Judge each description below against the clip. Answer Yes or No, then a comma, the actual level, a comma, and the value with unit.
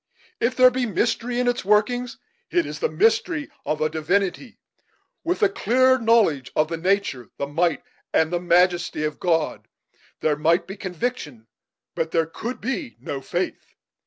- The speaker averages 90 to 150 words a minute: No, average, 160 wpm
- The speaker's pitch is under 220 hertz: Yes, high, 190 Hz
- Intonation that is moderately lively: No, wide, 7.6 semitones